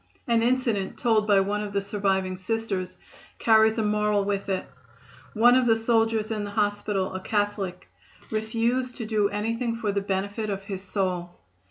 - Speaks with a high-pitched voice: Yes, high, 210 Hz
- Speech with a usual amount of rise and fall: No, narrow, 2.3 semitones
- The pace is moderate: Yes, average, 170 wpm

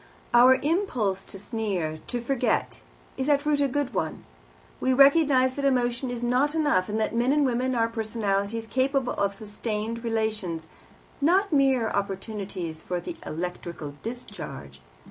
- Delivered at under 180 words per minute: Yes, average, 145 wpm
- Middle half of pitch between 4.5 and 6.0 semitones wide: Yes, average, 4.9 semitones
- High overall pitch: Yes, high, 235 Hz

